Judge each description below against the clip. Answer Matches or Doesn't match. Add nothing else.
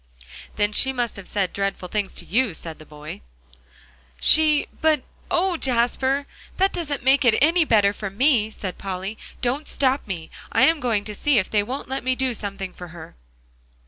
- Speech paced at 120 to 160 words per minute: Doesn't match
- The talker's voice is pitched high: Matches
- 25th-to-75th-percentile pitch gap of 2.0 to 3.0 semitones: Doesn't match